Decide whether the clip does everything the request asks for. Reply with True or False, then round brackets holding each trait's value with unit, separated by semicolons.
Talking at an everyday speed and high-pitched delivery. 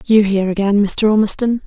True (180 wpm; 205 Hz)